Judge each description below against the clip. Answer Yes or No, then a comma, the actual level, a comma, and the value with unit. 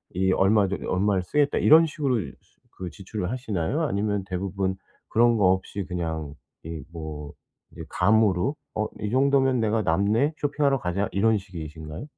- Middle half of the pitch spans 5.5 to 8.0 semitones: No, average, 5.1 semitones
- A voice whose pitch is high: No, low, 100 Hz